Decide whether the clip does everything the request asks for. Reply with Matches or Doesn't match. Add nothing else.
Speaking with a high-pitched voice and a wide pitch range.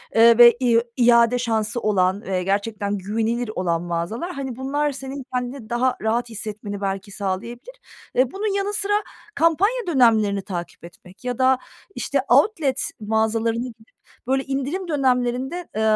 Doesn't match